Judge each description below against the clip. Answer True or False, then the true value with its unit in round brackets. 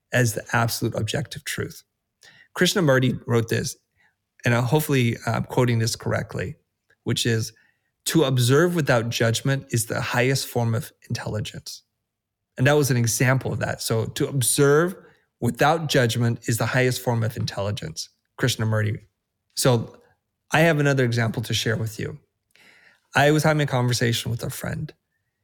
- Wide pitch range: False (3.7 semitones)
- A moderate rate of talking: True (145 wpm)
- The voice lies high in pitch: False (120 Hz)